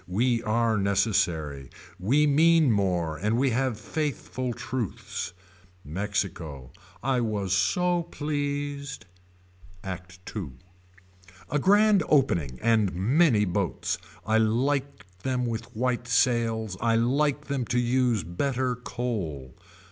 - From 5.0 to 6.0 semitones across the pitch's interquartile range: Yes, wide, 5.6 semitones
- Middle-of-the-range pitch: No, low, 115 Hz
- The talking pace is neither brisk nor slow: No, slow, 110 wpm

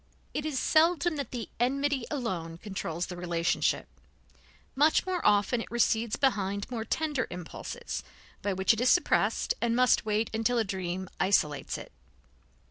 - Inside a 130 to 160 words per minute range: Yes, average, 150 wpm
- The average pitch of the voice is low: No, high, 225 Hz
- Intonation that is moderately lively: No, wide, 6.2 semitones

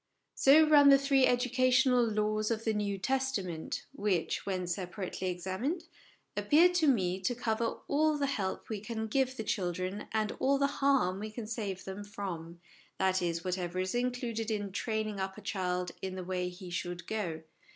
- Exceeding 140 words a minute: Yes, average, 175 wpm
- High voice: Yes, high, 210 Hz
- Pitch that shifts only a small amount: No, average, 5.3 semitones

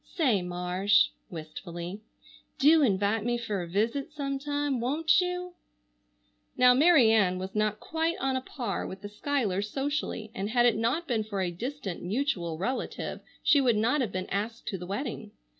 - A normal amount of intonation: No, wide, 6.2 semitones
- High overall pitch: Yes, high, 225 Hz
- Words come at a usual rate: Yes, average, 170 wpm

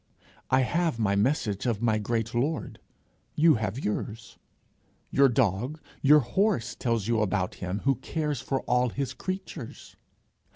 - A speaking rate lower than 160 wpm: Yes, average, 140 wpm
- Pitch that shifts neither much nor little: Yes, average, 4.6 semitones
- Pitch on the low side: Yes, low, 120 Hz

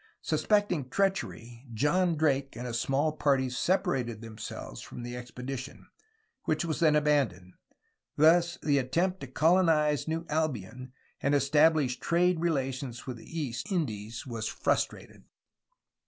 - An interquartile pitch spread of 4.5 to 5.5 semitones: Yes, average, 4.8 semitones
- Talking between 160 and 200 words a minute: No, slow, 135 wpm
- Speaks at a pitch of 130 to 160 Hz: Yes, medium, 140 Hz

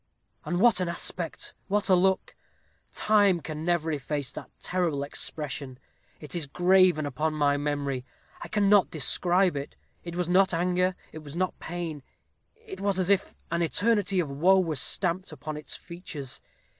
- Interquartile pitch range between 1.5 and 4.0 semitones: Yes, average, 3.6 semitones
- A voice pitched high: No, medium, 175 Hz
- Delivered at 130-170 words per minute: Yes, average, 160 wpm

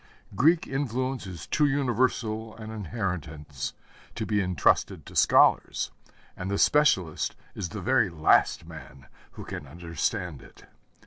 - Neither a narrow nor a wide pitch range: No, wide, 7.1 semitones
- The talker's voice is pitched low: Yes, low, 100 Hz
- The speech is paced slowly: Yes, slow, 130 wpm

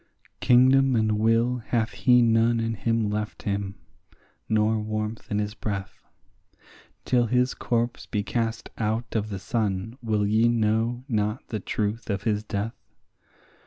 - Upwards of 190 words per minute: No, average, 145 wpm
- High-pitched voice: No, low, 110 Hz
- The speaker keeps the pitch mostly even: Yes, narrow, 1.9 semitones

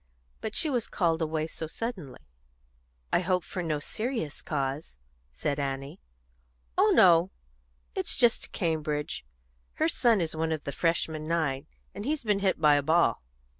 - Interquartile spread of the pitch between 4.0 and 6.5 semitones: Yes, average, 4.7 semitones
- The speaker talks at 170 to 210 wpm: No, average, 160 wpm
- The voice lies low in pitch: No, medium, 160 Hz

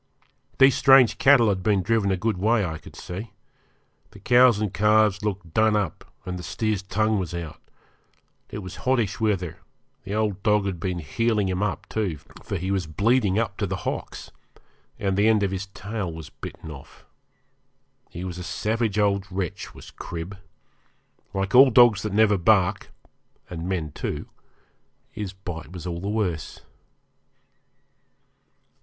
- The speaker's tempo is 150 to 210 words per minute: Yes, average, 160 wpm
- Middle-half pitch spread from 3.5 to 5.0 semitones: No, average, 3.1 semitones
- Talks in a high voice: No, low, 100 Hz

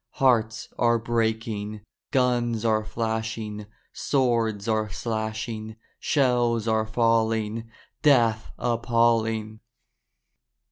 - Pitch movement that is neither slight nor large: No, narrow, 1.3 semitones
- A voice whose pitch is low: Yes, low, 115 Hz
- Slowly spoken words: Yes, slow, 80 wpm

